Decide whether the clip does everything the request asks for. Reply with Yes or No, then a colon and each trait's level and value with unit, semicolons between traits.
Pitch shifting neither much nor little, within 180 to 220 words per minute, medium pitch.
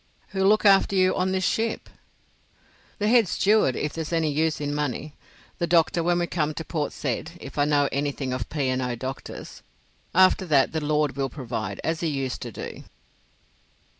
Yes: average, 4.3 semitones; average, 190 wpm; medium, 155 Hz